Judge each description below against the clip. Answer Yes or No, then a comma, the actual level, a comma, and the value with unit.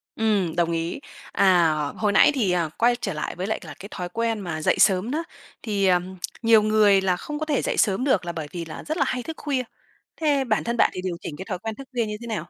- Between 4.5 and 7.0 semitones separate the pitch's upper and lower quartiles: Yes, average, 4.9 semitones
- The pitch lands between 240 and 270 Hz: No, high, 205 Hz